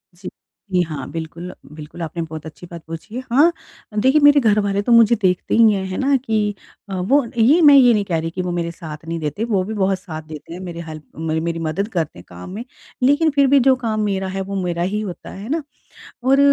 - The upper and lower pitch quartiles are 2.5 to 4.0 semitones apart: No, wide, 5.6 semitones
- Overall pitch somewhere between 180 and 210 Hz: Yes, high, 190 Hz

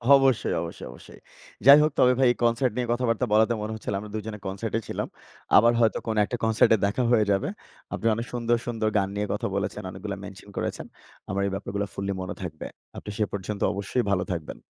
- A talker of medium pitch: No, low, 110 Hz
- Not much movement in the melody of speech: No, average, 3.0 semitones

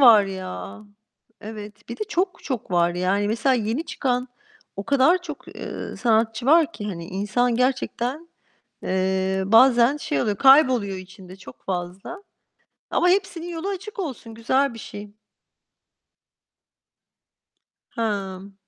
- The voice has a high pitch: Yes, high, 230 Hz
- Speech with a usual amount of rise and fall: No, wide, 6.2 semitones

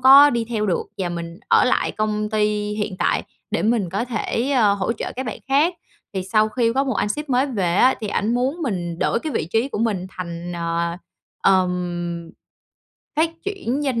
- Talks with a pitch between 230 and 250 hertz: No, high, 215 Hz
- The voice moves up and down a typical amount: No, wide, 5.8 semitones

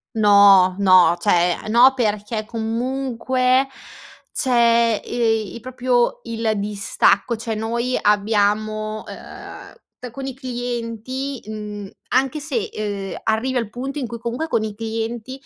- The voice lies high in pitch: Yes, high, 230 Hz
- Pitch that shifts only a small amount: No, average, 3.0 semitones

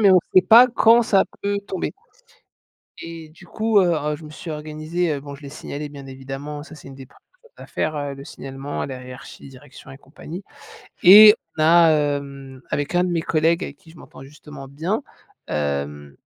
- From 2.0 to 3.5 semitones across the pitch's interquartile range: No, average, 4.0 semitones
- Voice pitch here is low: No, medium, 150 Hz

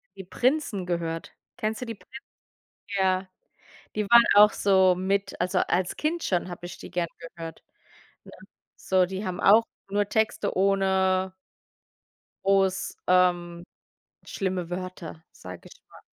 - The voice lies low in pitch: No, high, 190 Hz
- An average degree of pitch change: No, narrow, 2.0 semitones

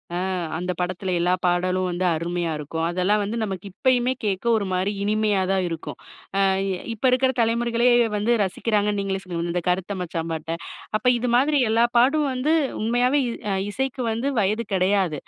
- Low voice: No, high, 200 Hz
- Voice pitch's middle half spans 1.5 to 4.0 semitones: No, average, 4.7 semitones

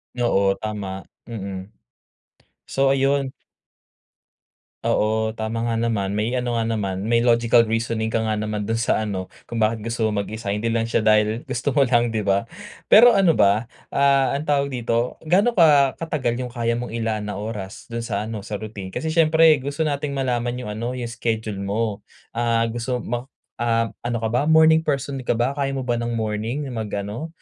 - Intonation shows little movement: No, average, 3.2 semitones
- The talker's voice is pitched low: Yes, low, 115 Hz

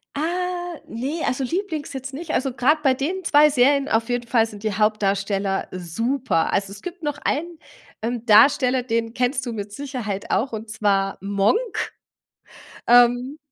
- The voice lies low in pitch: No, very high, 250 Hz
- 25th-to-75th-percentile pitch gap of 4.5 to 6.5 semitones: Yes, average, 5.3 semitones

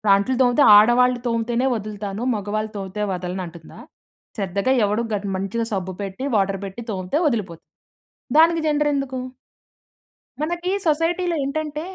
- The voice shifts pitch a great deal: Yes, wide, 6.3 semitones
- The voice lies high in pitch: Yes, high, 225 Hz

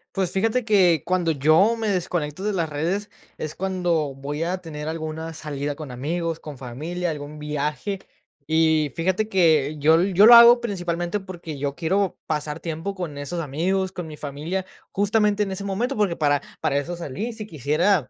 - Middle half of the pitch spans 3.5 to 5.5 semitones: Yes, average, 4.2 semitones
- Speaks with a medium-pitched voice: Yes, medium, 165 Hz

